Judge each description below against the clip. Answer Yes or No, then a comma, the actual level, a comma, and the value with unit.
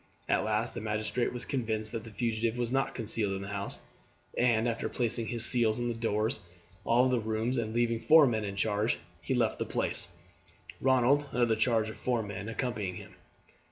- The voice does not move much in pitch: Yes, narrow, 2.0 semitones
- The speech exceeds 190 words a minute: Yes, average, 200 wpm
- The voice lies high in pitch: No, low, 115 Hz